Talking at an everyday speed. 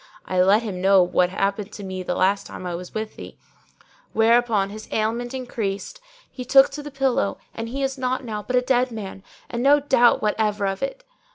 No: fast, 210 wpm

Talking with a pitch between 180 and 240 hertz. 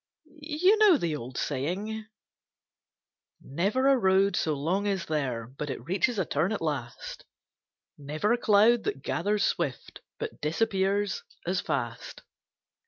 Yes: high, 190 Hz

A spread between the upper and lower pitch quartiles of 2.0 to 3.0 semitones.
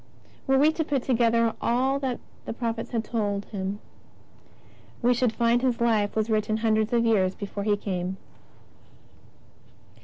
Yes: average, 2.7 semitones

